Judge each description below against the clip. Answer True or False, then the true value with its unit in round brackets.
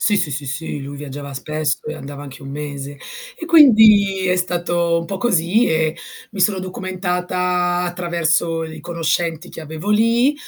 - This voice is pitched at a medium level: True (175 Hz)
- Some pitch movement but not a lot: True (3.4 semitones)